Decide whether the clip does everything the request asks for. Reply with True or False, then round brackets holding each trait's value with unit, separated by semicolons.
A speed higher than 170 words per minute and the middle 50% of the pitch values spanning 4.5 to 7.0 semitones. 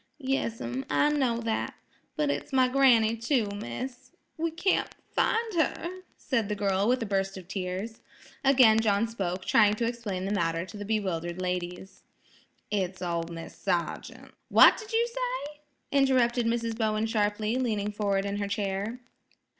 False (155 wpm; 4.8 semitones)